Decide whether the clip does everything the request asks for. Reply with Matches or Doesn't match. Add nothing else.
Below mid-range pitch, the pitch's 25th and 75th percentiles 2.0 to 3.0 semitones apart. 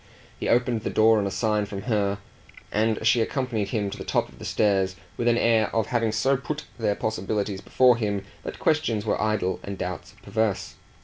Matches